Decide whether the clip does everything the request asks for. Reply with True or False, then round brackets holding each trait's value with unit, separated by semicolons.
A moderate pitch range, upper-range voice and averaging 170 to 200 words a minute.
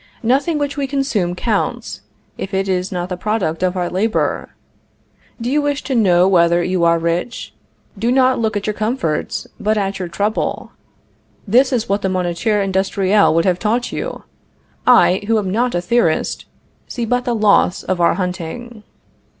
True (4.8 semitones; 200 Hz; 175 wpm)